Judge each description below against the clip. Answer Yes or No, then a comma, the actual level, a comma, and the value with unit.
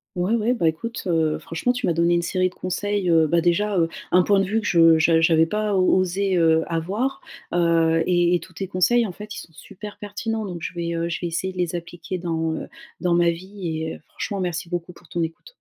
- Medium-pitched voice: Yes, medium, 175 Hz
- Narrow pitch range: No, average, 3.0 semitones